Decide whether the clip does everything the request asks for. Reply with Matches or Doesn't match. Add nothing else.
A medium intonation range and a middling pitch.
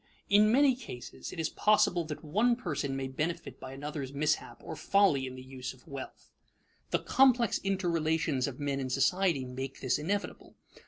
Doesn't match